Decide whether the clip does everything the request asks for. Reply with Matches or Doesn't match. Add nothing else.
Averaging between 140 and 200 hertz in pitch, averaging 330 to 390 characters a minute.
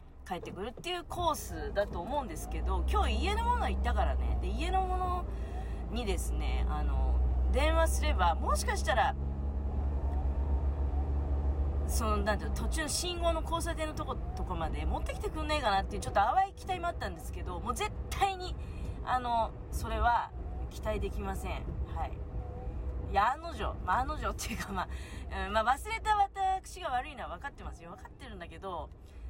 Doesn't match